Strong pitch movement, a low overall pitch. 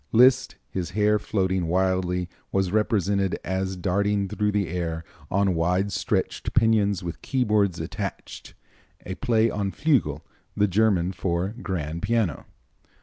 No: average, 2.7 semitones; very low, 95 Hz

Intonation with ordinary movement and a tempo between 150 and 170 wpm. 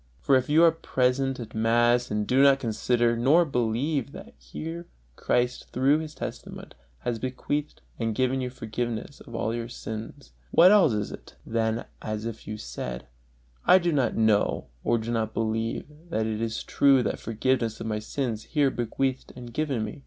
No: average, 3.3 semitones; average, 180 wpm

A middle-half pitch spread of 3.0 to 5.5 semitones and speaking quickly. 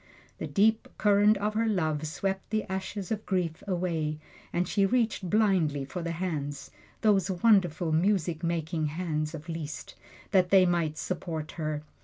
No: average, 4.1 semitones; average, 155 wpm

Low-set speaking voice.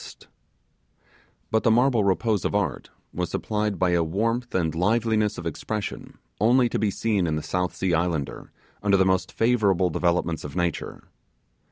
Yes: very low, 95 Hz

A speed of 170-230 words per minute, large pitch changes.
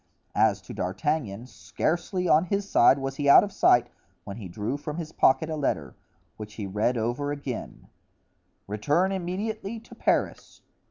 No: average, 160 wpm; wide, 7.7 semitones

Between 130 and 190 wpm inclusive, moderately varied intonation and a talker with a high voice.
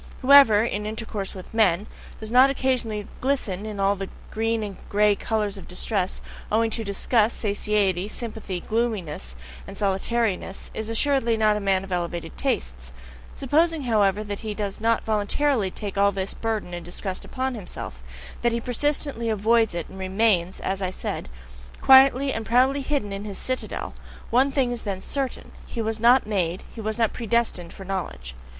Yes: average, 170 wpm; average, 3.4 semitones; high, 215 Hz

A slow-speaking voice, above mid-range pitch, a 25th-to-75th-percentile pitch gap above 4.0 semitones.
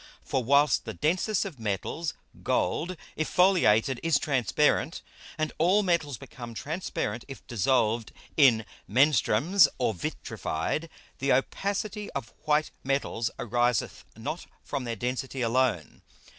No: slow, 120 wpm; low, 135 Hz; wide, 5.4 semitones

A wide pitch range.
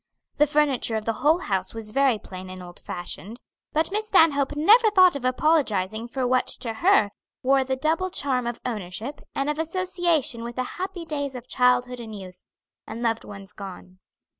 Yes: wide, 6.0 semitones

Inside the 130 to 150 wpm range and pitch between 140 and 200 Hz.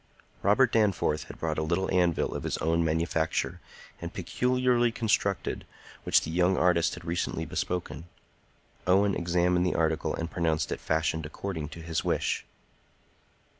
No: average, 145 wpm; very low, 85 Hz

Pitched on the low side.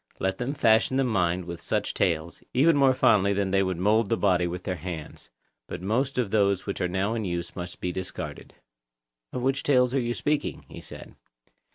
Yes: low, 100 Hz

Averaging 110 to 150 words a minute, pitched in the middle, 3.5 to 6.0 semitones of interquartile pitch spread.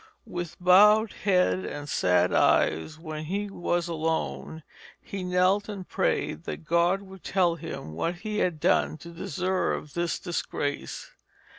No: average, 140 wpm; medium, 175 Hz; average, 3.1 semitones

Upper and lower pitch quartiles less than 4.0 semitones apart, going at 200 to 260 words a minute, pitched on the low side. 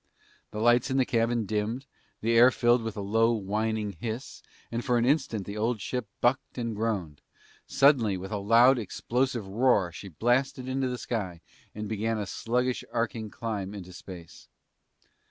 No: average, 3.0 semitones; average, 175 wpm; low, 115 Hz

